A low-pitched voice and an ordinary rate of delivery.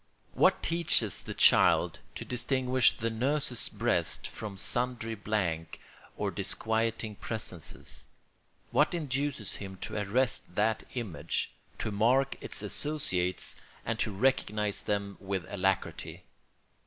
No: low, 110 Hz; slow, 115 wpm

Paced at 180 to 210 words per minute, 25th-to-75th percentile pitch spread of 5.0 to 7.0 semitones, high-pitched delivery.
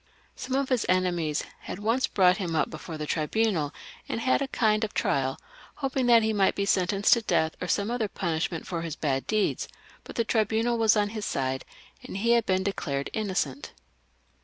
Yes: average, 195 wpm; wide, 5.6 semitones; high, 200 Hz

